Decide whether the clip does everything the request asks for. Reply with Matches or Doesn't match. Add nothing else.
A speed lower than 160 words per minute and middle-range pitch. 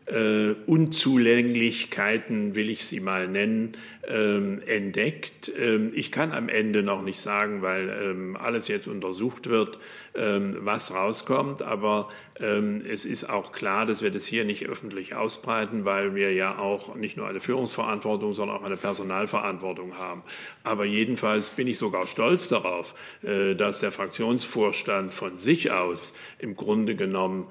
Doesn't match